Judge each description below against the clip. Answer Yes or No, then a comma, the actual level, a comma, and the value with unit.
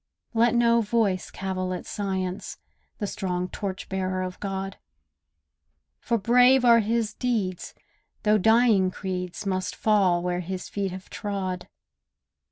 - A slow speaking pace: Yes, slow, 130 wpm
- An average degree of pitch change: Yes, average, 3.2 semitones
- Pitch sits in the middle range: No, high, 195 Hz